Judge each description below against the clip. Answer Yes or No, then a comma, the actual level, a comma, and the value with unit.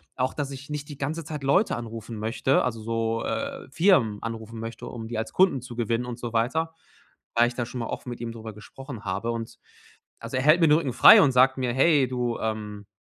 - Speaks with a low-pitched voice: Yes, low, 120 Hz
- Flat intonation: No, average, 3.3 semitones